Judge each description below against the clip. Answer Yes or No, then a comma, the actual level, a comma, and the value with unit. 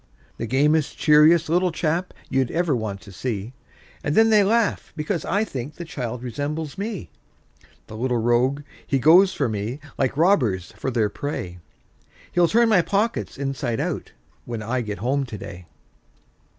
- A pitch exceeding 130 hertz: Yes, medium, 140 Hz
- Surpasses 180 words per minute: No, average, 165 wpm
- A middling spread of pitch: No, wide, 6.5 semitones